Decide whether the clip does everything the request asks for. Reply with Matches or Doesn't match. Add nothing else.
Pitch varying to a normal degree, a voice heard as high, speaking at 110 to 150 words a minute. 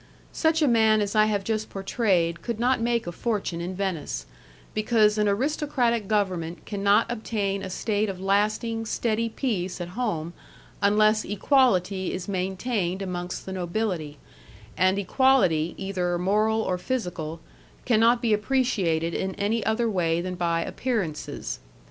Matches